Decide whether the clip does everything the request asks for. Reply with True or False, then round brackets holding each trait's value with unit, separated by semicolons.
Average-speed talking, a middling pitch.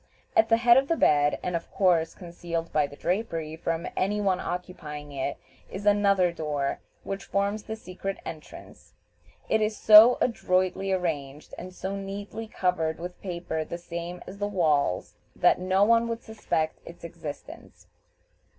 True (160 wpm; 180 Hz)